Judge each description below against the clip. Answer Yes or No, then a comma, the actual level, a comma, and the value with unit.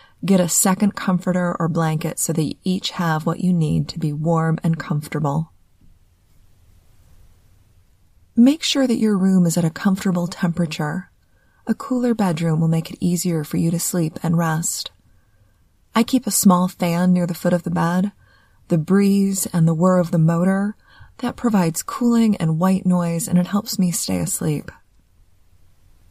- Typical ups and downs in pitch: Yes, average, 4.2 semitones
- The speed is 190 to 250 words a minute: No, average, 170 wpm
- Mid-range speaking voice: Yes, medium, 170 Hz